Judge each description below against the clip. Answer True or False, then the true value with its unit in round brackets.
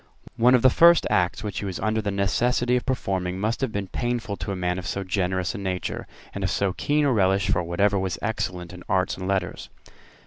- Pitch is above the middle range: False (100 Hz)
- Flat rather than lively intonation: False (3.8 semitones)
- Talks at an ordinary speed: False (230 wpm)